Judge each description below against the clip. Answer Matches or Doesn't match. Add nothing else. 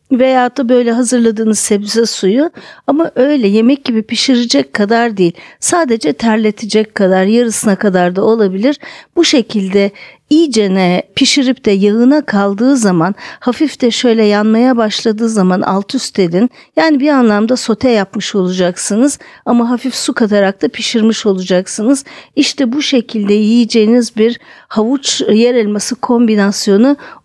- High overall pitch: Matches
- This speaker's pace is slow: Doesn't match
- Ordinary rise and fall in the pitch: Matches